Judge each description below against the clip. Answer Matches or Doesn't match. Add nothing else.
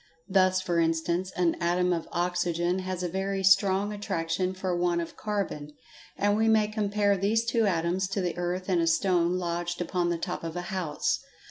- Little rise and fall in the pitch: Matches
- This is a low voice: Doesn't match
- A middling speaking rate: Matches